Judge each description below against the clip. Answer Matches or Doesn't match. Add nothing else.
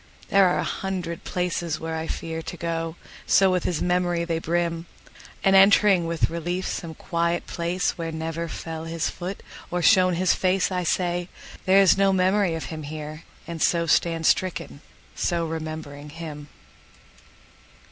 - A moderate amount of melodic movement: Doesn't match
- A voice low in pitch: Doesn't match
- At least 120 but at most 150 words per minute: Matches